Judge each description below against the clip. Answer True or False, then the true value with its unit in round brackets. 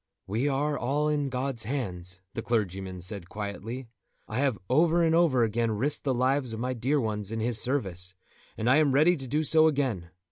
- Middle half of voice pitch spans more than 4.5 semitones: True (5.0 semitones)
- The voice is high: False (125 Hz)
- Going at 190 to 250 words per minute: True (200 wpm)